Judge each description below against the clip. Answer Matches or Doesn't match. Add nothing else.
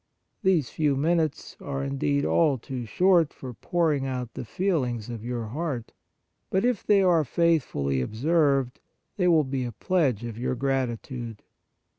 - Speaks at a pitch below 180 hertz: Matches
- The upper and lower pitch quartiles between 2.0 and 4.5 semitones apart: Doesn't match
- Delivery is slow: Doesn't match